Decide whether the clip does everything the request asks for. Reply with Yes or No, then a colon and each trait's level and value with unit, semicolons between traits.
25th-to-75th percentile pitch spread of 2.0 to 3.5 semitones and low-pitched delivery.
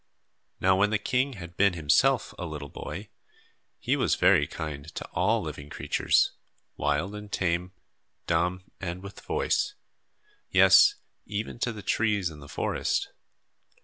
No: average, 4.7 semitones; very low, 90 Hz